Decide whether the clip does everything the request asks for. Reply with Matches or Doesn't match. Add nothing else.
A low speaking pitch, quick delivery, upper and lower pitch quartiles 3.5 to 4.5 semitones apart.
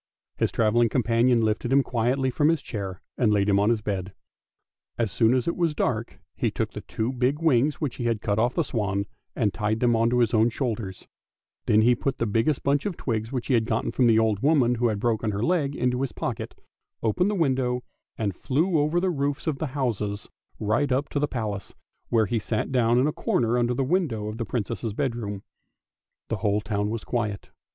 Matches